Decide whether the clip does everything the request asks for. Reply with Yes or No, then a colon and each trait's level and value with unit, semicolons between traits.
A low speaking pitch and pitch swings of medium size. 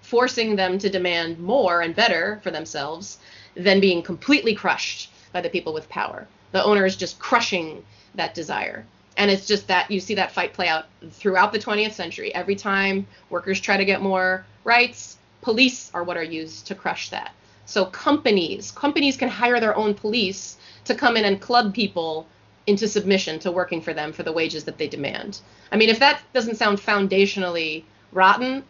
No: high, 195 Hz; average, 3.9 semitones